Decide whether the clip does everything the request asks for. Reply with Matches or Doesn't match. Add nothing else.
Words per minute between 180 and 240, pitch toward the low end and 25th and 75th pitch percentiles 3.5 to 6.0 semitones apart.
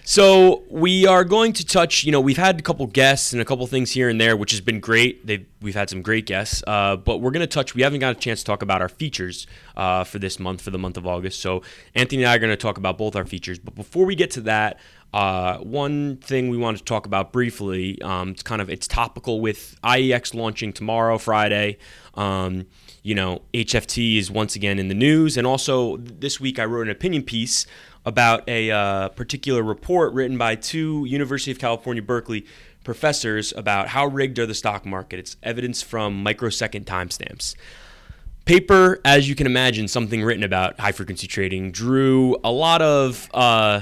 Matches